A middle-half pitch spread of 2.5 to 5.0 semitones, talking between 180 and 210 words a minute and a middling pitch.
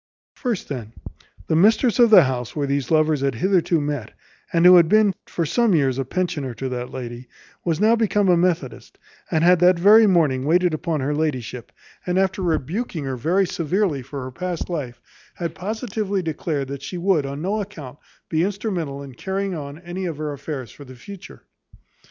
No: wide, 5.4 semitones; average, 190 wpm; medium, 165 Hz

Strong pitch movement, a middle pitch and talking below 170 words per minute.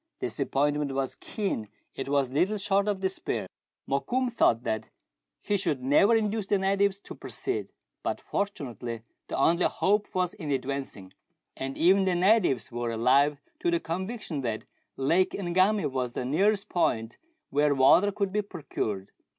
Yes: wide, 6.9 semitones; medium, 170 Hz; average, 150 wpm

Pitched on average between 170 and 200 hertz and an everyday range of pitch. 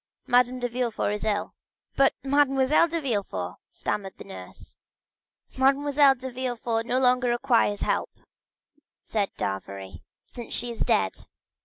No: high, 245 Hz; average, 4.2 semitones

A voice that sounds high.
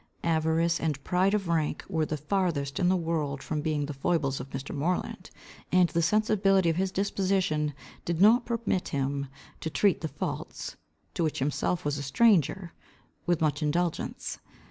No: medium, 165 Hz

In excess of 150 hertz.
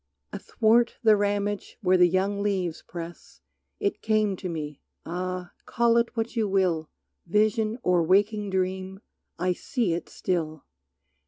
Yes: high, 190 Hz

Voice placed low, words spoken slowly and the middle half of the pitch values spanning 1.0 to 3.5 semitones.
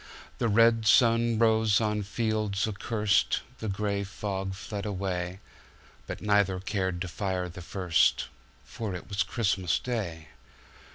Yes: low, 100 Hz; slow, 115 wpm; average, 2.7 semitones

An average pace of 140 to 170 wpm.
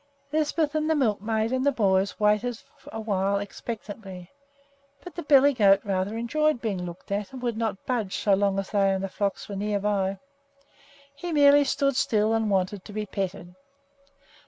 No: average, 180 wpm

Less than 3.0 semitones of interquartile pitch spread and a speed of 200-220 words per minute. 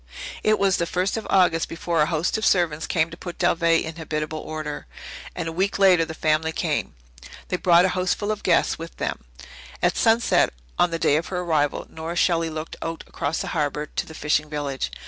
Yes: narrow, 2.5 semitones; fast, 205 wpm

